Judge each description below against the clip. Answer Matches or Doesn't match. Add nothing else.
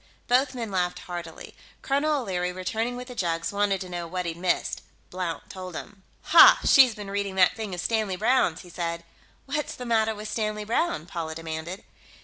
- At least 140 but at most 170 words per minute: Doesn't match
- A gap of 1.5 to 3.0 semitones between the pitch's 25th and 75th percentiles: Doesn't match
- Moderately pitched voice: Doesn't match